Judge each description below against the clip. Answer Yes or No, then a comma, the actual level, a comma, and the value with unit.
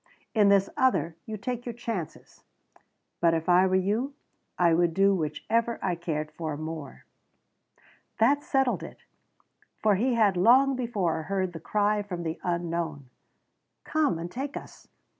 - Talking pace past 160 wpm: No, average, 155 wpm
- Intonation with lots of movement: Yes, wide, 5.8 semitones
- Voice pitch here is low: No, high, 190 Hz